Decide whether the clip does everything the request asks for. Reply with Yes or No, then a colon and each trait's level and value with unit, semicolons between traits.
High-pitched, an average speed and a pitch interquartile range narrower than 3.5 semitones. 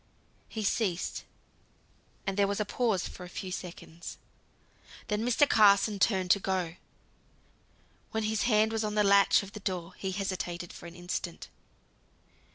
Yes: high, 200 Hz; average, 155 wpm; average, 2.8 semitones